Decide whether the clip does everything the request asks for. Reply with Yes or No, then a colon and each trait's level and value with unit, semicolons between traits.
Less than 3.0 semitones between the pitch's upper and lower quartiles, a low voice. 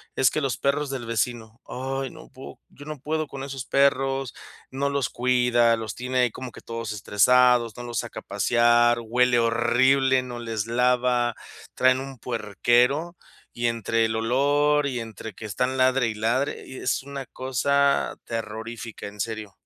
Yes: narrow, 2.5 semitones; low, 125 Hz